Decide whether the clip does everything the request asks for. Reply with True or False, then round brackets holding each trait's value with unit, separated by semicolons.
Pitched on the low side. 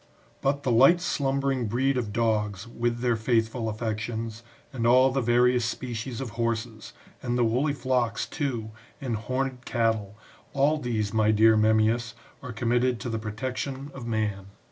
True (120 Hz)